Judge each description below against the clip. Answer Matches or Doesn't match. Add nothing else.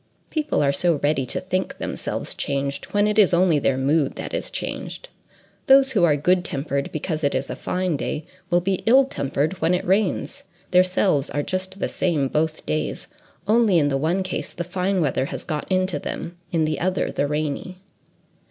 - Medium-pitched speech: Matches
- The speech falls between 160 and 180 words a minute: Doesn't match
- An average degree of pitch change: Matches